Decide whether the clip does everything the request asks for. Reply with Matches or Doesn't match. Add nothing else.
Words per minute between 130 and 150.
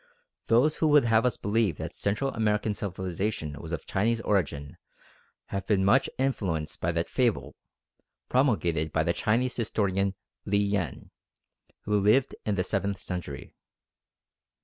Matches